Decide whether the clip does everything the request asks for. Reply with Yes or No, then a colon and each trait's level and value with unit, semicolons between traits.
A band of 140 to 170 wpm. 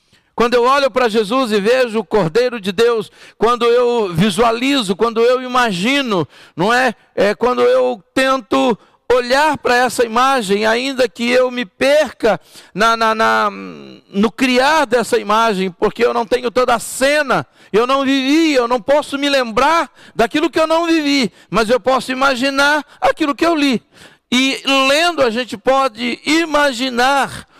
Yes: average, 160 wpm